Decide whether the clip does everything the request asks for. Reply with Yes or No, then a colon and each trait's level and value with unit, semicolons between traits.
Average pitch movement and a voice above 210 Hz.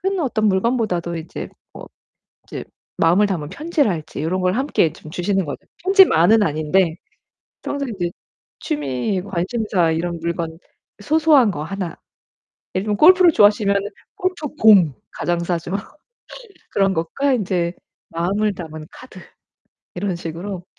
No: average, 4.5 semitones; high, 190 Hz